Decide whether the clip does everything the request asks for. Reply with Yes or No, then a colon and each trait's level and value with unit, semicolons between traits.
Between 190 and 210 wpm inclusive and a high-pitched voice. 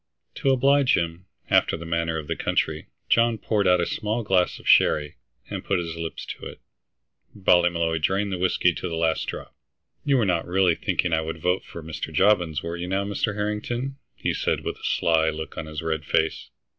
No: fast, 205 wpm; very low, 90 Hz